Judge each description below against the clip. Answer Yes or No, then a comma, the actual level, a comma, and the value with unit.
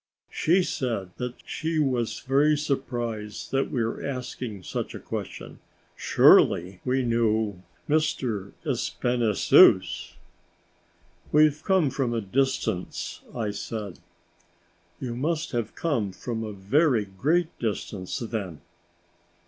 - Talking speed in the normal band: No, slow, 110 wpm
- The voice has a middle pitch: No, low, 120 Hz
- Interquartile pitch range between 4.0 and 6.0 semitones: Yes, average, 5.0 semitones